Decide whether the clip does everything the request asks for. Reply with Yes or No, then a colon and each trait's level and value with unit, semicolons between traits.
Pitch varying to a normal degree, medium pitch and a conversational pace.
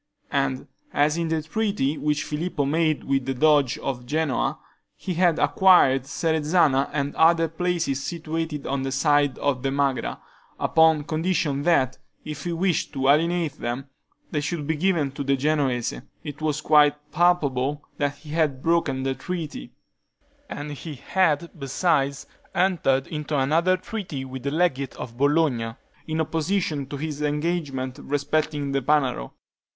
Yes: average, 3.0 semitones; medium, 150 Hz; average, 145 wpm